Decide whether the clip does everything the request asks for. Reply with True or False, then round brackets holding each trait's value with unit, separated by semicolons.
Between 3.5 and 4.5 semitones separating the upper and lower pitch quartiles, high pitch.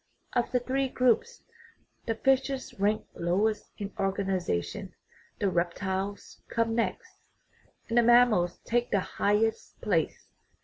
True (3.9 semitones; 220 Hz)